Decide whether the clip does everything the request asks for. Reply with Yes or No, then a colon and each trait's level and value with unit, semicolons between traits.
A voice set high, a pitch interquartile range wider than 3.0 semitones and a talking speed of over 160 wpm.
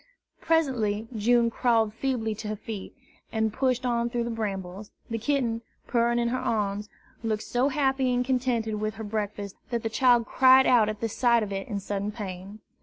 No: high, 225 Hz; average, 2.7 semitones; average, 185 wpm